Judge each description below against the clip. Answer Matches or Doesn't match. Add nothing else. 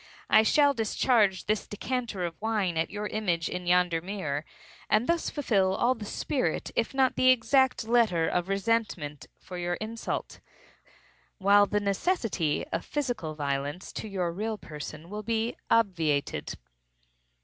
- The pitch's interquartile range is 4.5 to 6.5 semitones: Matches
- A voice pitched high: Matches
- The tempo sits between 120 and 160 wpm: Matches